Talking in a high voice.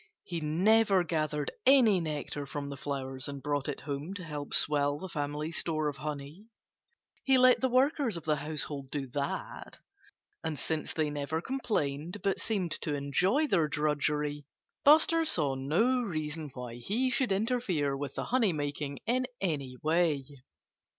No: medium, 155 Hz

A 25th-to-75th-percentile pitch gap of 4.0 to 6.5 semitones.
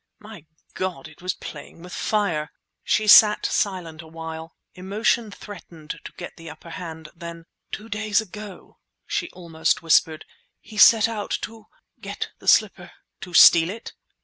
Yes: average, 4.4 semitones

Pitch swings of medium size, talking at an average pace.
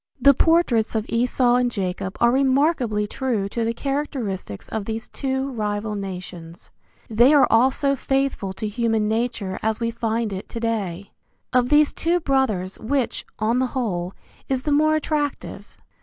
Yes: average, 4.3 semitones; average, 155 wpm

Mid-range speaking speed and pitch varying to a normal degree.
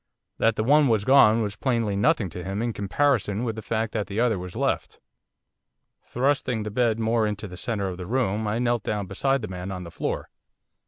No: fast, 215 wpm; average, 3.2 semitones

